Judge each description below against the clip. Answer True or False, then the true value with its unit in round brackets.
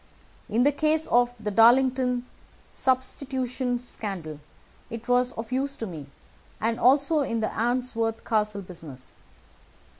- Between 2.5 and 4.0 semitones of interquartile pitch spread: True (2.9 semitones)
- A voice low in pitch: False (245 Hz)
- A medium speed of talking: False (125 wpm)